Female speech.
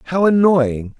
No: male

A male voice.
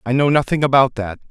Yes: male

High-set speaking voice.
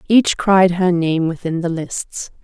No: medium, 180 Hz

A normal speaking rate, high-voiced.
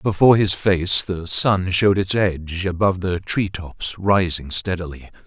No: average, 160 wpm; very low, 90 Hz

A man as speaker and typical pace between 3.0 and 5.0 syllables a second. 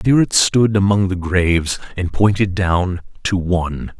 Yes: male; 4.5 syllables/s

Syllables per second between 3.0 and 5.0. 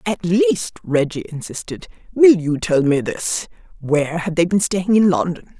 Yes: 4.4 syllables/s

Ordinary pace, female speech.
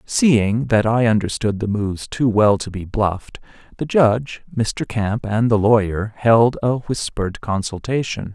No: average, 160 wpm; male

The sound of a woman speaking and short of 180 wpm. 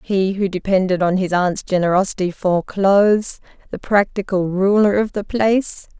Yes: female; average, 150 wpm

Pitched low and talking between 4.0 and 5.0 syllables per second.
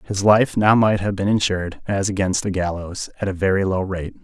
No: low, 100 Hz; 5.4 syllables/s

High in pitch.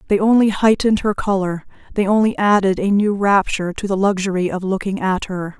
Yes: high, 195 Hz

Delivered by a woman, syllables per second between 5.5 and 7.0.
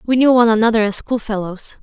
Yes: female; 6.4 syllables/s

